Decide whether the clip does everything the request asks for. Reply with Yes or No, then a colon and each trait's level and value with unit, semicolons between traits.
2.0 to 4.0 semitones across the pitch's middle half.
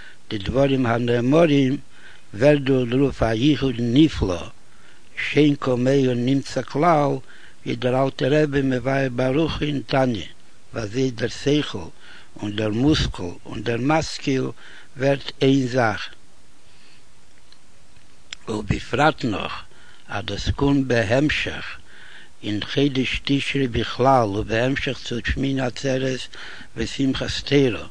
Yes: average, 3.4 semitones